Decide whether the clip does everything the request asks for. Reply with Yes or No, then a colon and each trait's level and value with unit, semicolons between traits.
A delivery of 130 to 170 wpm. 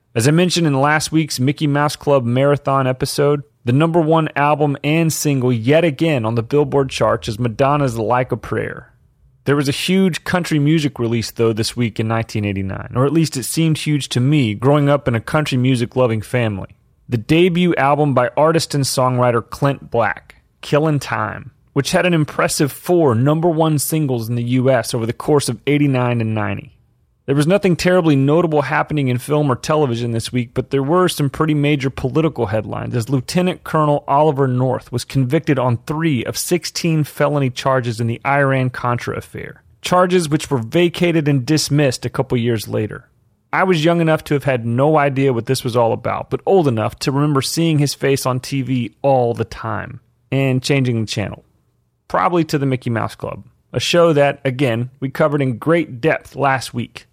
No: average, 190 wpm